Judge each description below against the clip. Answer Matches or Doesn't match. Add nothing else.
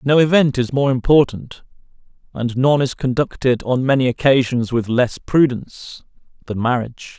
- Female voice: Doesn't match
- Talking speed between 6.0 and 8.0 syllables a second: Doesn't match